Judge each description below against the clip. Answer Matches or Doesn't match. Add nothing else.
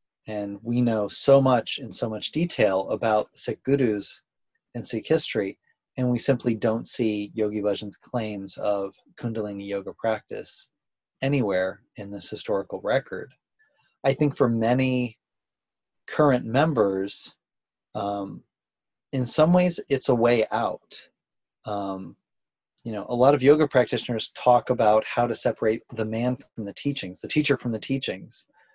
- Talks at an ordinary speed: Matches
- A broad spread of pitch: Doesn't match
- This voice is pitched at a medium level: Doesn't match